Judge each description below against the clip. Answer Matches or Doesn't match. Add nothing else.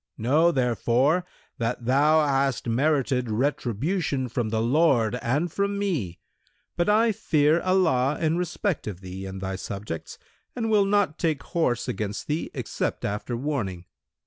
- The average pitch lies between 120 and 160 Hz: Matches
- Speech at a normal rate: Matches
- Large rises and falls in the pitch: Matches